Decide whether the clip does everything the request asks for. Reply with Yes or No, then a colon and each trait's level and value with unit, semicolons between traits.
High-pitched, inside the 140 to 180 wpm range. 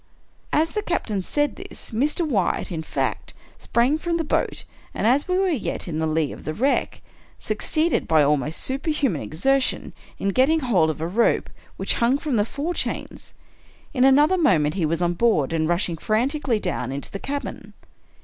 No: high, 235 Hz; average, 190 wpm